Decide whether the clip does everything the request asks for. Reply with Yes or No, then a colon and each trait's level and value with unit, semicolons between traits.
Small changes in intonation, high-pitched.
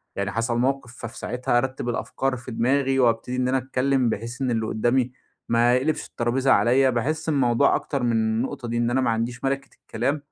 No: narrow, 2.1 semitones; low, 125 Hz